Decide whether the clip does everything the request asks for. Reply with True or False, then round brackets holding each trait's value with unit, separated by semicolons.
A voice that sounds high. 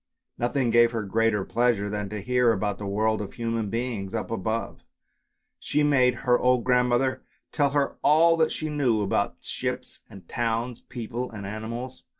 False (115 Hz)